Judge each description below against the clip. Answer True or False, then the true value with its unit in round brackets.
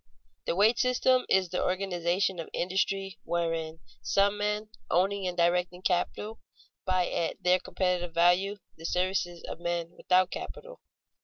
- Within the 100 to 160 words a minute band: True (140 wpm)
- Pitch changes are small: True (2.2 semitones)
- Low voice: False (185 Hz)